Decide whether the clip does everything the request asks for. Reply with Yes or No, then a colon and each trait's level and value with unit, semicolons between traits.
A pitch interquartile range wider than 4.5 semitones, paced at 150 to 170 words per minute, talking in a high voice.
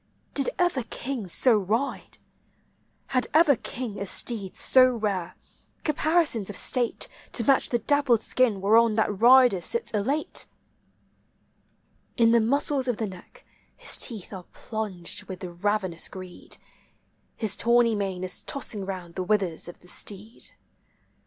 No: average, 4.9 semitones; average, 140 wpm; high, 220 Hz